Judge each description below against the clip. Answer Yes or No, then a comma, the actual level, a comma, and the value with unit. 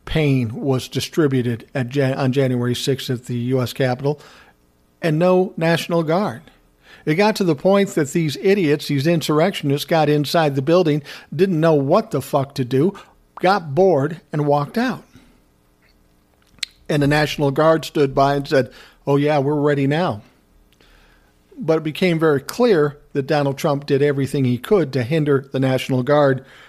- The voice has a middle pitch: Yes, medium, 145 Hz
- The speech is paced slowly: No, average, 160 wpm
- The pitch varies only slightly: No, average, 3.7 semitones